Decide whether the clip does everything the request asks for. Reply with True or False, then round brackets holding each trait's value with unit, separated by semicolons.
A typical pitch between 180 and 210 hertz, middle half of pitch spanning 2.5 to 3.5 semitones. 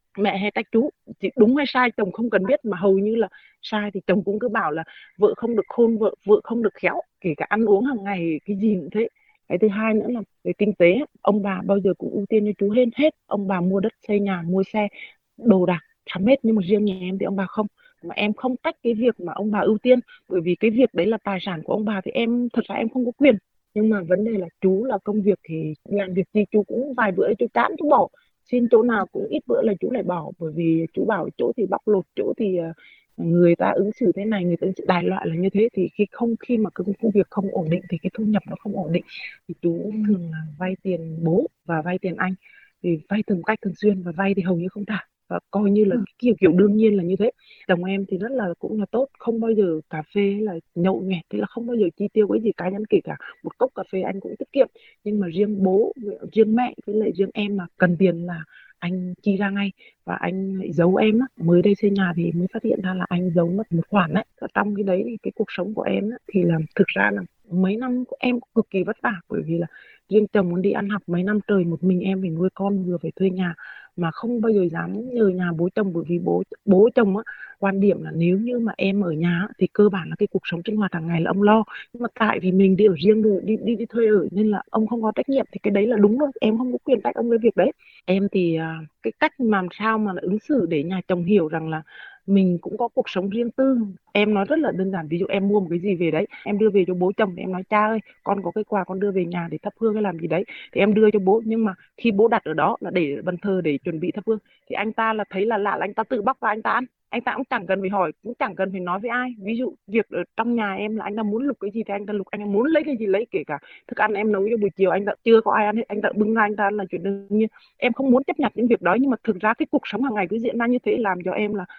True (205 Hz; 3.2 semitones)